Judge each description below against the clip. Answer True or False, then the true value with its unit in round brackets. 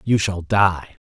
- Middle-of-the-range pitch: False (95 Hz)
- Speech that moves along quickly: False (170 wpm)